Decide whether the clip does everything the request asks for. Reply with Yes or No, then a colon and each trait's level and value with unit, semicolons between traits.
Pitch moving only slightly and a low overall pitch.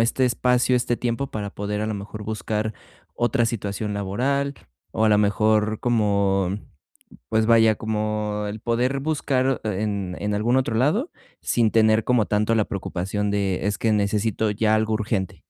Yes: narrow, 2.3 semitones; low, 110 Hz